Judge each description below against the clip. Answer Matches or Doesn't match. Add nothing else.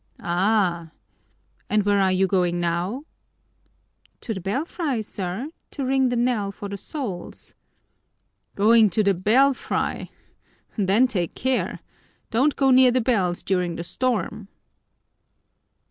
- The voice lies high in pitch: Matches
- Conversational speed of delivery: Doesn't match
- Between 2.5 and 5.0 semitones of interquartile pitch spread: Doesn't match